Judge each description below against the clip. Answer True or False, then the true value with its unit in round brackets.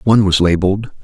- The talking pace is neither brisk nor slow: True (175 wpm)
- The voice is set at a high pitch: False (95 Hz)